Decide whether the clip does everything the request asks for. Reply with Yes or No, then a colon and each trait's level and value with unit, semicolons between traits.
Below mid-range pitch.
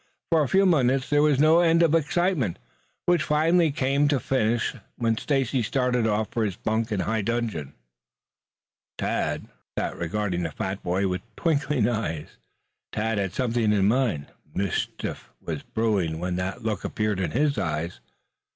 Yes: low, 115 Hz